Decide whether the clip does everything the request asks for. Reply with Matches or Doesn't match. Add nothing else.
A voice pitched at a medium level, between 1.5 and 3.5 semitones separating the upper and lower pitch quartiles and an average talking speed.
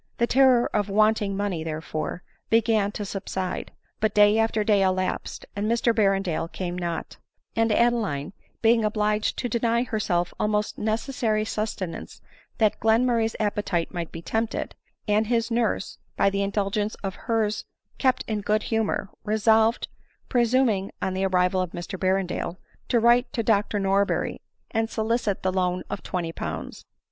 Doesn't match